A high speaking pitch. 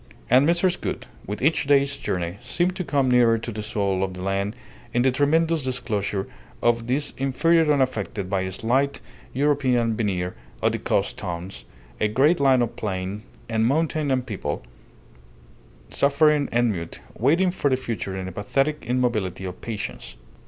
No: low, 120 Hz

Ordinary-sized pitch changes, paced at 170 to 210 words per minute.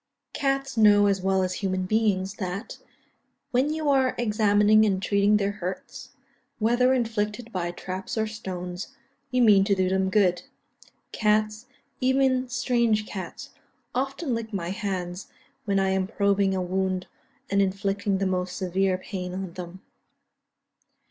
No: average, 3.1 semitones; average, 150 wpm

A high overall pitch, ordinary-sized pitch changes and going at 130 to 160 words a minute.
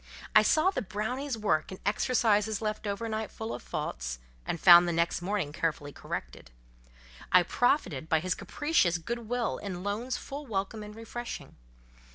Yes: high, 210 Hz; average, 4.9 semitones; average, 155 wpm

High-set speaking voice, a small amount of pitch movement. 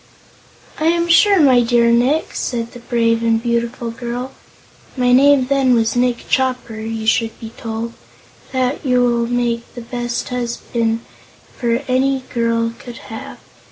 Yes: high, 240 Hz; narrow, 1.6 semitones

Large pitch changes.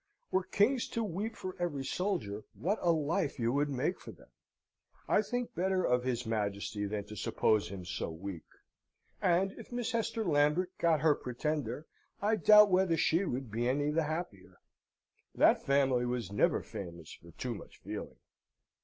Yes: wide, 8.1 semitones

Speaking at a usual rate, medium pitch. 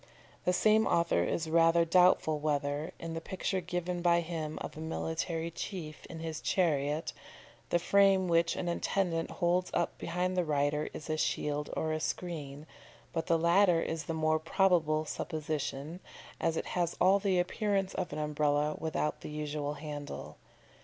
Yes: average, 165 wpm; medium, 165 Hz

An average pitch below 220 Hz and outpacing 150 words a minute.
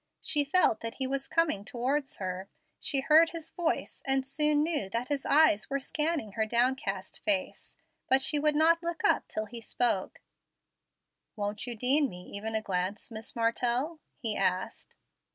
No: very high, 260 Hz; average, 170 wpm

